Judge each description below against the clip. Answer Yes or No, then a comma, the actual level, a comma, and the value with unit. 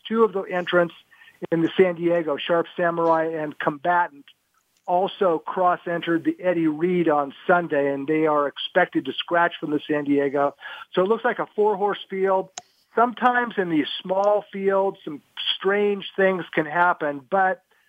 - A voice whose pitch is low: No, medium, 175 Hz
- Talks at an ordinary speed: Yes, average, 165 wpm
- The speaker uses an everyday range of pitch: Yes, average, 3.3 semitones